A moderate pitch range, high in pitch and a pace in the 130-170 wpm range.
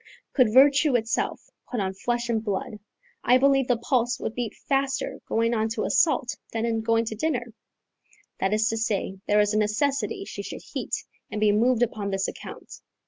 No: average, 3.0 semitones; high, 230 Hz; average, 190 wpm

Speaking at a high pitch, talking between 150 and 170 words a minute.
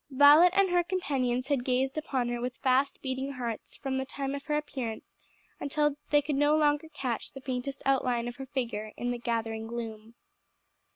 No: very high, 265 Hz; average, 185 wpm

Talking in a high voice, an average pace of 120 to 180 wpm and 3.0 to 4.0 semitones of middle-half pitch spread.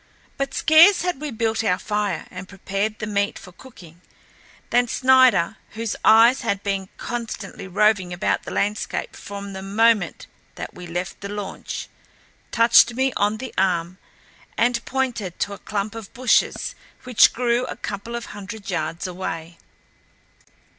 Yes: high, 210 Hz; average, 150 wpm; average, 3.7 semitones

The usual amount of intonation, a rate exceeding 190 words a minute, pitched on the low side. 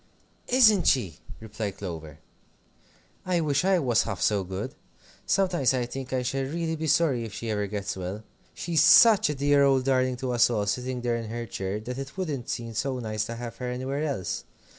Yes: average, 4.8 semitones; average, 200 wpm; low, 125 Hz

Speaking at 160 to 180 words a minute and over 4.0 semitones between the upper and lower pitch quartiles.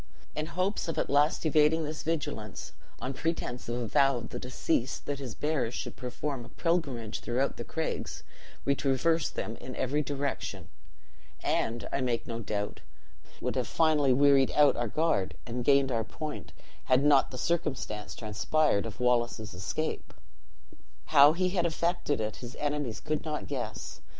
Yes: average, 165 wpm; average, 4.4 semitones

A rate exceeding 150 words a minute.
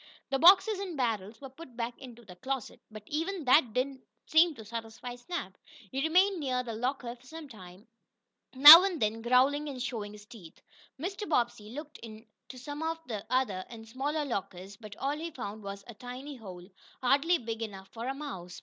Yes: average, 195 wpm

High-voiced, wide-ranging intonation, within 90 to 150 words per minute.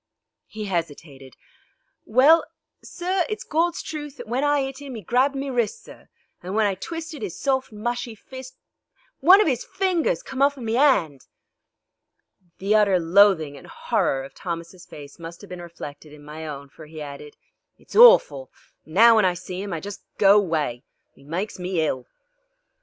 No: high, 205 Hz; wide, 8.8 semitones; average, 180 wpm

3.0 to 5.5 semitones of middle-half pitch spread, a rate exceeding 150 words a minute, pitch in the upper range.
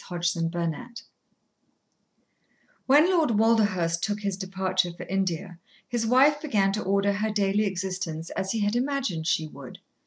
No: average, 4.1 semitones; average, 145 wpm; high, 195 Hz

